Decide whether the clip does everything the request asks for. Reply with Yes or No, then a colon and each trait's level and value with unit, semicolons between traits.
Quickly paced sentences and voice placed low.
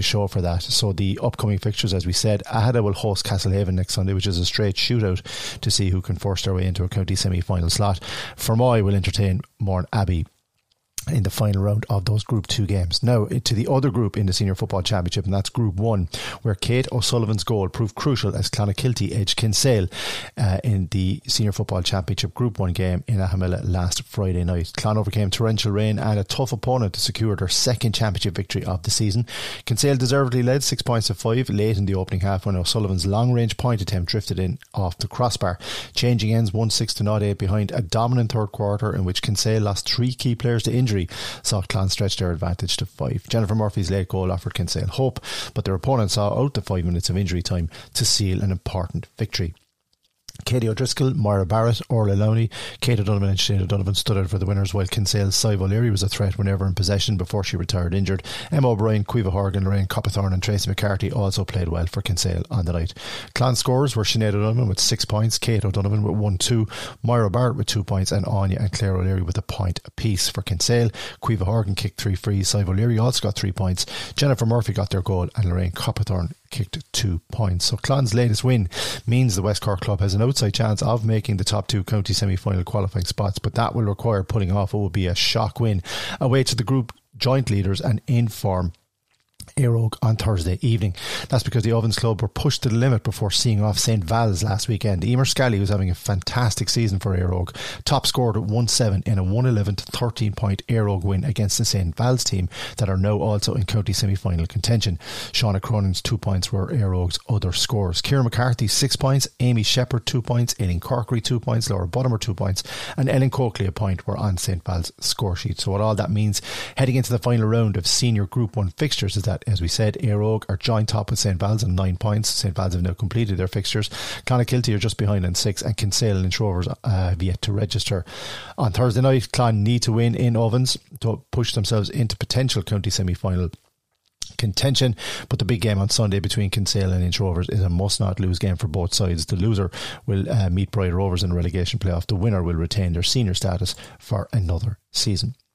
Yes: fast, 215 wpm; low, 105 Hz